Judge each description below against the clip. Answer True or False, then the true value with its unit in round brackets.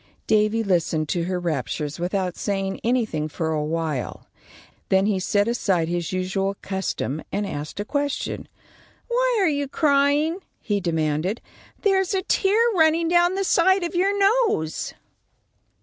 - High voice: True (205 Hz)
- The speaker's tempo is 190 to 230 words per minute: False (140 wpm)